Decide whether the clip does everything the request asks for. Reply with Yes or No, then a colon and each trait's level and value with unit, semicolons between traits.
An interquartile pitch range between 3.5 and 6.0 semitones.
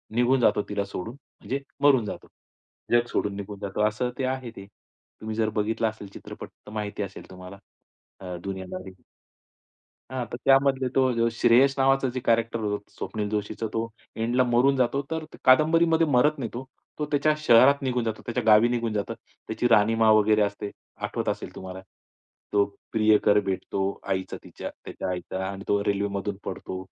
Yes: average, 4.0 semitones